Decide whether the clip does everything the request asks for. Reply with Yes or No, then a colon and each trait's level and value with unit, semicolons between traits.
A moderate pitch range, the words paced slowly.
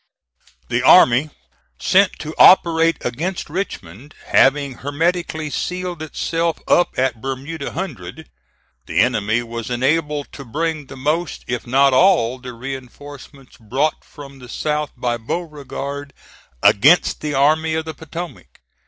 Yes: average, 4.2 semitones; slow, 125 wpm